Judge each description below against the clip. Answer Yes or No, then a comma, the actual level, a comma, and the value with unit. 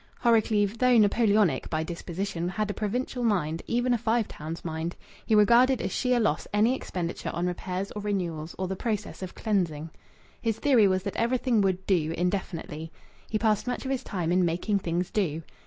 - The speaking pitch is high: Yes, high, 200 Hz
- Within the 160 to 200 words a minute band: Yes, average, 185 wpm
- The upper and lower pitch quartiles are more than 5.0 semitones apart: No, average, 4.6 semitones